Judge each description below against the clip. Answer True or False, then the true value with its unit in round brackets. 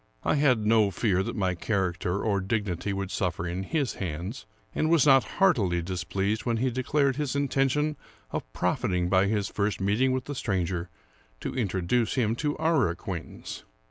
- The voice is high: False (105 Hz)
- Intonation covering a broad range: True (5.9 semitones)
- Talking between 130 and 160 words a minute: False (175 wpm)